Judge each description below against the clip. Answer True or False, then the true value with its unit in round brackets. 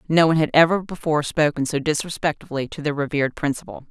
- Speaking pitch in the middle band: True (150 Hz)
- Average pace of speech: True (185 wpm)